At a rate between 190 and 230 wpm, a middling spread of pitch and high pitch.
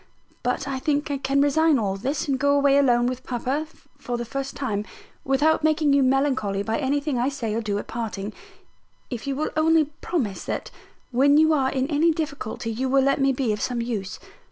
Yes: fast, 205 wpm; average, 3.2 semitones; very high, 270 Hz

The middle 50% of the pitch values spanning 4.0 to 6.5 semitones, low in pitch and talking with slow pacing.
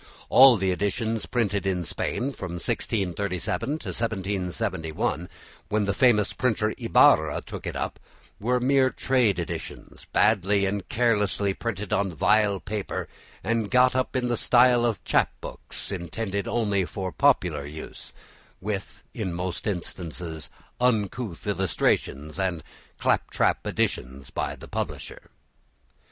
Yes: average, 4.3 semitones; low, 100 Hz; slow, 130 wpm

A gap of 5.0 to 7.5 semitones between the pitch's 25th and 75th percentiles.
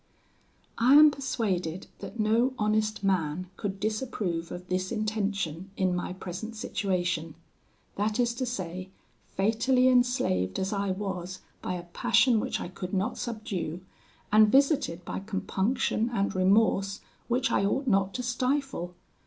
No: average, 4.3 semitones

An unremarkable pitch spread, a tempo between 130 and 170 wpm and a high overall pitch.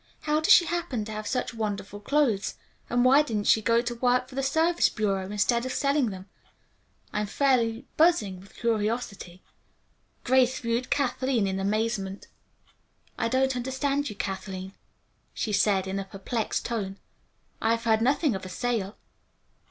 Yes: average, 4.4 semitones; average, 160 wpm; high, 230 Hz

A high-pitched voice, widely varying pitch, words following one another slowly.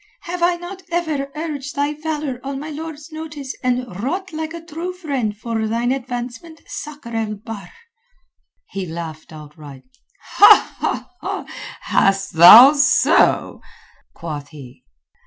Yes: very high, 270 Hz; wide, 7.0 semitones; slow, 120 wpm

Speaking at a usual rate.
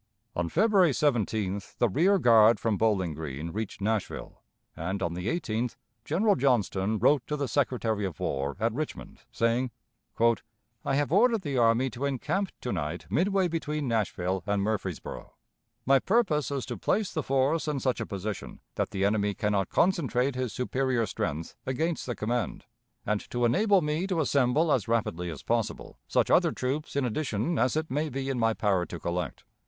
Yes: average, 175 wpm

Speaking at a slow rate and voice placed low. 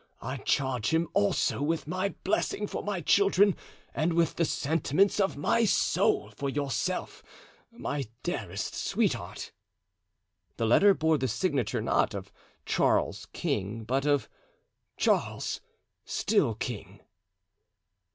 No: slow, 115 wpm; medium, 160 Hz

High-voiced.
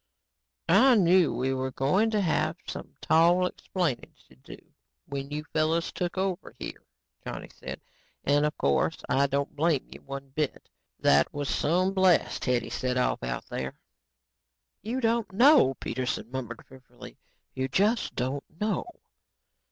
No: medium, 150 Hz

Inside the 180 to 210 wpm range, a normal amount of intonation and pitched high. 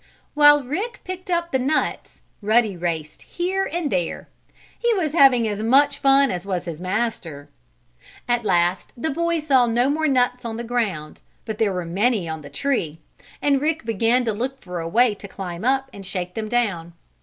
No: average, 190 wpm; wide, 7.1 semitones; high, 235 Hz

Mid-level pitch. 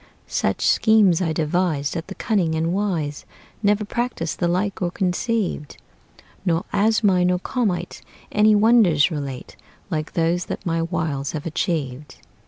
Yes: medium, 175 Hz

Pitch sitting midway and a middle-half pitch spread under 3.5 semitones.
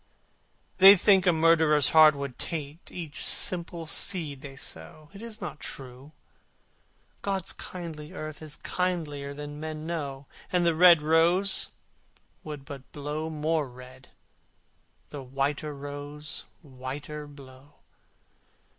Yes: medium, 150 Hz; average, 2.8 semitones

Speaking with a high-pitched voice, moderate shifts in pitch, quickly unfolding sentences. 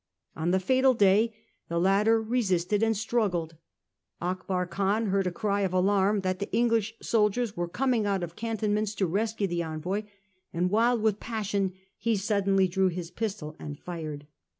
No: high, 200 Hz; average, 3.4 semitones; average, 165 wpm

